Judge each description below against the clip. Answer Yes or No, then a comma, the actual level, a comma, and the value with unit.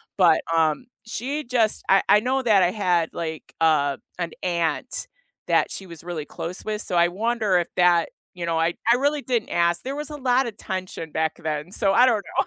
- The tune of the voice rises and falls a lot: Yes, wide, 5.9 semitones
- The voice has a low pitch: No, medium, 185 Hz